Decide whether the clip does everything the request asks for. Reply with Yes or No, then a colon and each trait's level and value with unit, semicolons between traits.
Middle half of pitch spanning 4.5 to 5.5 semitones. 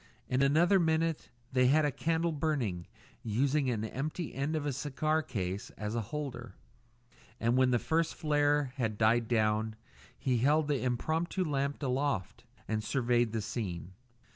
Yes: average, 4.8 semitones